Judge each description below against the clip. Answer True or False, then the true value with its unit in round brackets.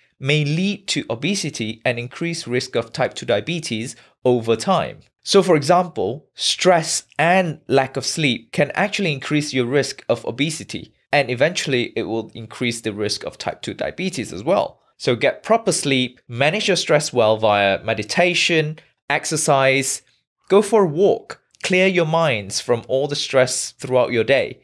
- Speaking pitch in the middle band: True (145 Hz)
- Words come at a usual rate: True (160 wpm)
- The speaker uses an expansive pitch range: True (5.7 semitones)